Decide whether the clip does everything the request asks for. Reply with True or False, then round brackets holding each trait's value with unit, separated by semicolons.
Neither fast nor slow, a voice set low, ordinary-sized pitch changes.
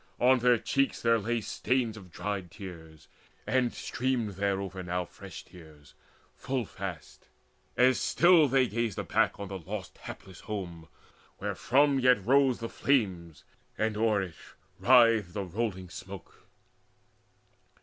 False (130 wpm; 105 Hz; 5.0 semitones)